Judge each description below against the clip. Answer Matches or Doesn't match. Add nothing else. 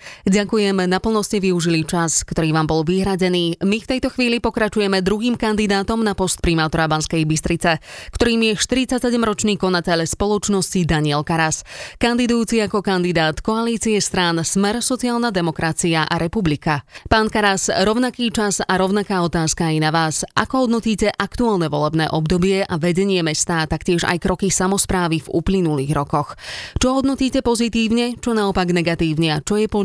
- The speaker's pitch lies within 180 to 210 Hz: Matches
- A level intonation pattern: Doesn't match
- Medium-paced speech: Matches